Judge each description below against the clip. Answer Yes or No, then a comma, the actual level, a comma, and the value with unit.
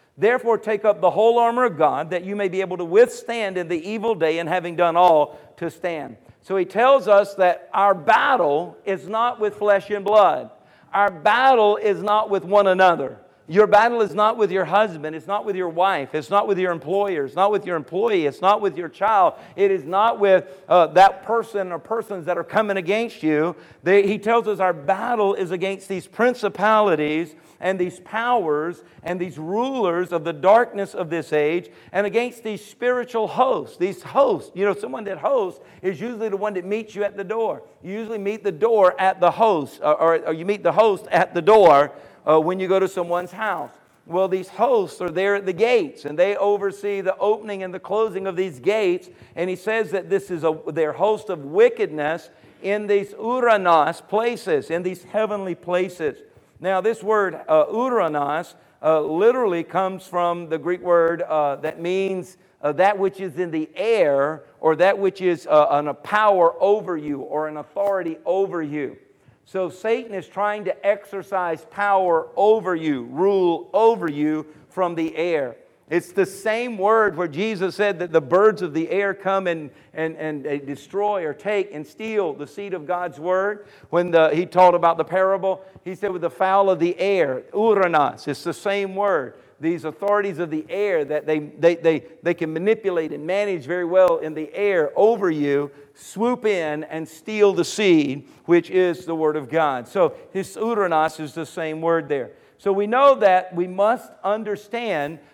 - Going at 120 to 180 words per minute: No, average, 190 wpm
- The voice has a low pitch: No, high, 190 Hz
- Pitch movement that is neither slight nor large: Yes, average, 3.8 semitones